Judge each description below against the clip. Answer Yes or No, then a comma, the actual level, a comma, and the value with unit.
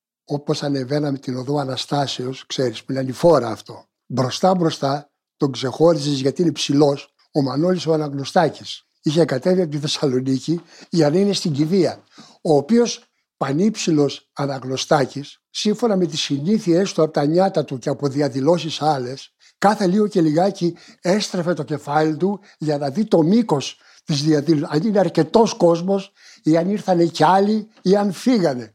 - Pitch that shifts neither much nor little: Yes, average, 4.6 semitones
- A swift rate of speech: No, average, 155 wpm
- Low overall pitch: No, medium, 155 Hz